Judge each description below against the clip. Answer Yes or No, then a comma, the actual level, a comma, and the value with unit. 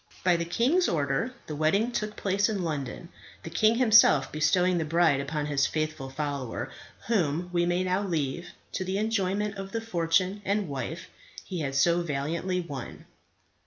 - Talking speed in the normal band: Yes, average, 165 wpm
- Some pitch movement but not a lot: Yes, average, 4.7 semitones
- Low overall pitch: No, medium, 175 Hz